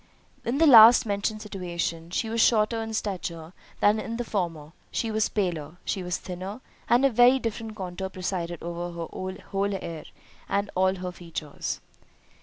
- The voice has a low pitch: No, high, 190 Hz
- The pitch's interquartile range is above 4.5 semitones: No, average, 4.1 semitones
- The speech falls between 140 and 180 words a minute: Yes, average, 150 wpm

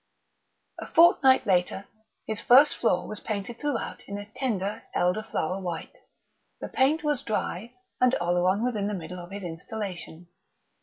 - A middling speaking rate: Yes, average, 155 wpm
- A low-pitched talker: No, high, 205 Hz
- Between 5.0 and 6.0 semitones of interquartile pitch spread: Yes, average, 5.3 semitones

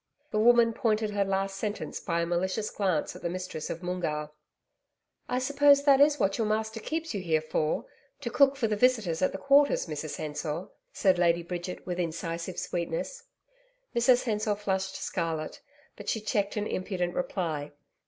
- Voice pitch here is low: No, high, 190 Hz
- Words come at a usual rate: Yes, average, 175 wpm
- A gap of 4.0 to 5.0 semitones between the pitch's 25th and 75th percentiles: Yes, average, 4.6 semitones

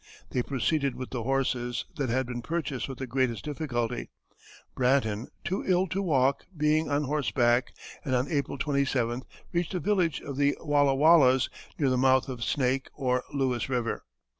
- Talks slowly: No, average, 165 wpm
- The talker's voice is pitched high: No, low, 135 Hz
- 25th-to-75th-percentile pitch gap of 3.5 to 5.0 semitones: No, average, 2.8 semitones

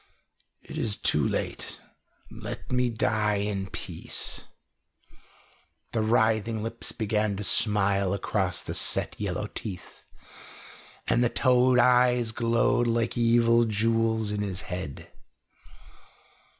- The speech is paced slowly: Yes, slow, 110 wpm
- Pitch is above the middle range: No, low, 110 Hz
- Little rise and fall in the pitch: Yes, narrow, 2.2 semitones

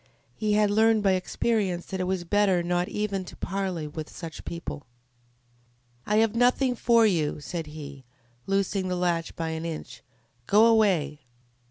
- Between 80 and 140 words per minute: No, average, 160 wpm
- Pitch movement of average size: Yes, average, 4.0 semitones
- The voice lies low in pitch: No, medium, 185 Hz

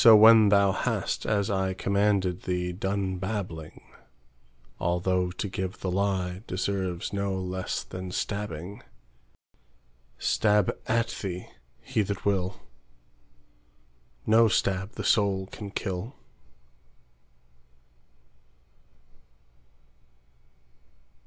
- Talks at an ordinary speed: No, slow, 75 wpm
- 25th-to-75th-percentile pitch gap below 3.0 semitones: Yes, narrow, 2.4 semitones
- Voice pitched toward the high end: No, very low, 95 Hz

